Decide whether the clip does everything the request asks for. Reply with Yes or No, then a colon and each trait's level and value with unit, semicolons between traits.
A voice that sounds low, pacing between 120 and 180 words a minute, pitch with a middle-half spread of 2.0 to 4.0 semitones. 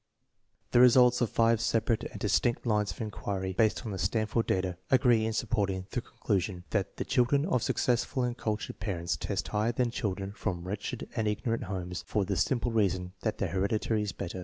No: low, 110 Hz; average, 195 wpm; average, 3.6 semitones